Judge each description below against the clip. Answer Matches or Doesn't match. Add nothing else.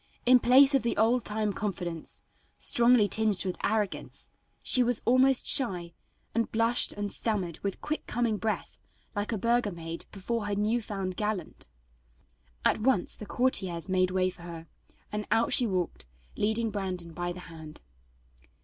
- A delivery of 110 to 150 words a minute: Doesn't match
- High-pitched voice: Matches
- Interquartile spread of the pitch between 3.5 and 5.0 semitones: Matches